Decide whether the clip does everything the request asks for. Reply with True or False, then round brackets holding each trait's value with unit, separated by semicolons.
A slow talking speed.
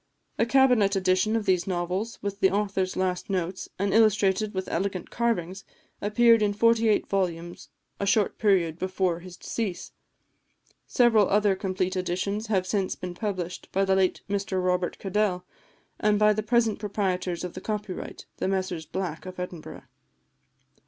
False (155 wpm)